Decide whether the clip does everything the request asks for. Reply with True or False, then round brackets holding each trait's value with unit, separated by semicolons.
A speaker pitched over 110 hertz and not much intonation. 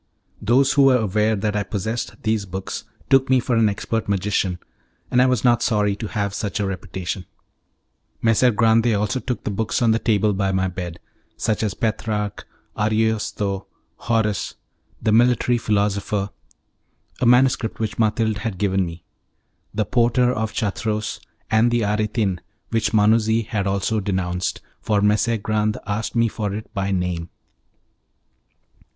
False (105 Hz; 2.2 semitones)